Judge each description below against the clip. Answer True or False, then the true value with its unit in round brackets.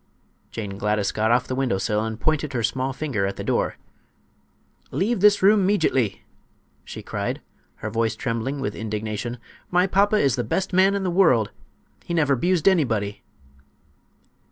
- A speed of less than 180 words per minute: True (160 wpm)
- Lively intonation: True (8.5 semitones)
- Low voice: True (130 Hz)